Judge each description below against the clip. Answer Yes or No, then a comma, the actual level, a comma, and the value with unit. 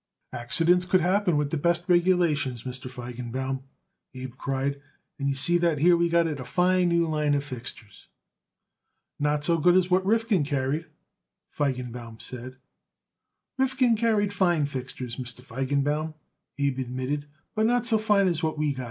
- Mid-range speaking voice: Yes, medium, 150 Hz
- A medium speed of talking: Yes, average, 160 wpm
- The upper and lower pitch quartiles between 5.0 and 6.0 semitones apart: Yes, average, 5.3 semitones